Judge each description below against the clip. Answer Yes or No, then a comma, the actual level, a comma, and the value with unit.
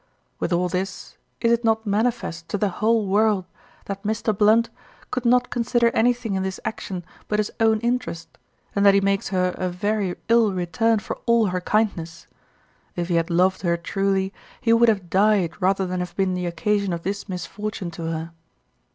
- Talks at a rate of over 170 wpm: Yes, average, 185 wpm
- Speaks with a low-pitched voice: No, high, 200 Hz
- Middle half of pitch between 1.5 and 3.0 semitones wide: No, average, 3.5 semitones